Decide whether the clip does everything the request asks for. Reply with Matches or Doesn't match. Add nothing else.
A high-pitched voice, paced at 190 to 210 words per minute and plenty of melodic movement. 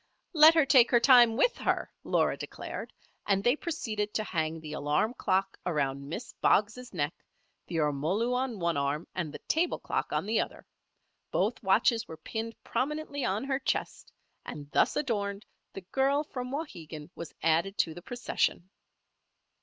Doesn't match